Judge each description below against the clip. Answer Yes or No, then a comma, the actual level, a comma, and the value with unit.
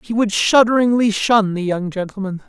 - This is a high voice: Yes, high, 210 Hz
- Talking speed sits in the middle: Yes, average, 170 wpm